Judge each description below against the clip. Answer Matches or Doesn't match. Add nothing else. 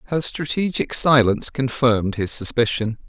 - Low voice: Matches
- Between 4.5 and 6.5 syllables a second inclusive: Matches